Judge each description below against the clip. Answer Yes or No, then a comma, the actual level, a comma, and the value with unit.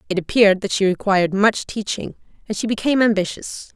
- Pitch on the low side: No, high, 205 Hz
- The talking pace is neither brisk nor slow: Yes, average, 175 wpm